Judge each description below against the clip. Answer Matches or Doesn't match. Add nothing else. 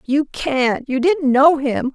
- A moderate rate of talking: Matches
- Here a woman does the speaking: Matches